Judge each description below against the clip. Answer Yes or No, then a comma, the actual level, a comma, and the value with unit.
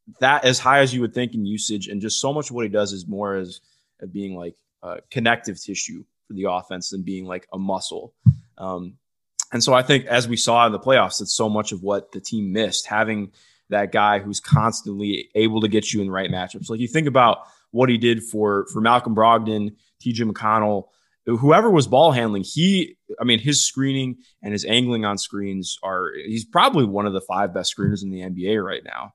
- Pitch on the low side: Yes, low, 110 Hz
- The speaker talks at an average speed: No, fast, 220 wpm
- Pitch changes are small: No, average, 3.5 semitones